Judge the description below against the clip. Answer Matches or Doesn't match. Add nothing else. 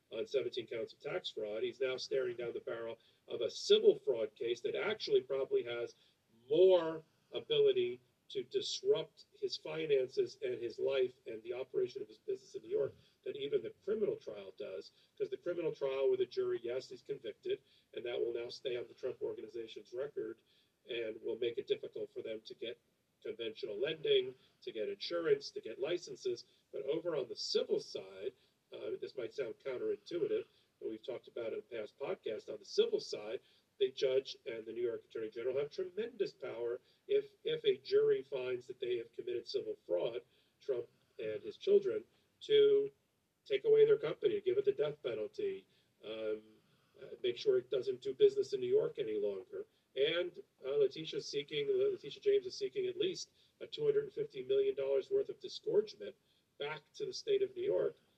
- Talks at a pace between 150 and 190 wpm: Matches